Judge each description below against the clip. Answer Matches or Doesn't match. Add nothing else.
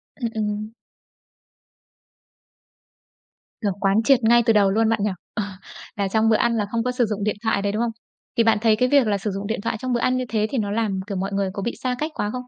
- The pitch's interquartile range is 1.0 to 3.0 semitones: Matches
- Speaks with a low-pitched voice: Doesn't match